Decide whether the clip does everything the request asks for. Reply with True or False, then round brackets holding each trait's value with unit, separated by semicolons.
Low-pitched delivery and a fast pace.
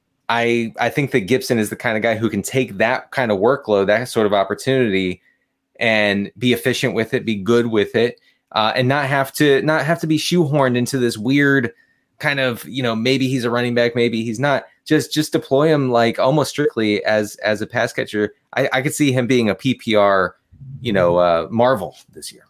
True (125 Hz; 215 wpm)